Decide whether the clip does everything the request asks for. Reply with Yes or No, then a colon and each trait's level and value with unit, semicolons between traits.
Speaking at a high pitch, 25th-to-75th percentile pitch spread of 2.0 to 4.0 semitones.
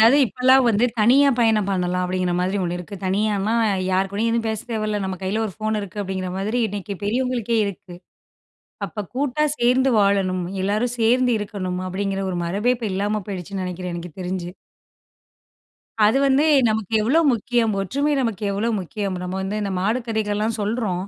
Yes: high, 205 Hz; average, 3.4 semitones